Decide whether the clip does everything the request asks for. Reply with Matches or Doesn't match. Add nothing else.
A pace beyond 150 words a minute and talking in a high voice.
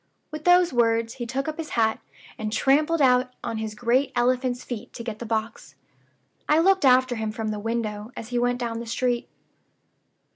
Matches